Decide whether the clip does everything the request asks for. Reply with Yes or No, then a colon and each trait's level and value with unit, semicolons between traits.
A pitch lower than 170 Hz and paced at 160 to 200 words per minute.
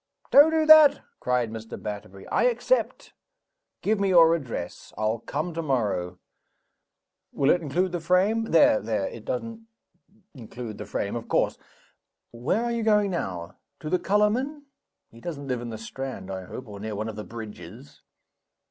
Yes: low, 135 Hz; average, 165 wpm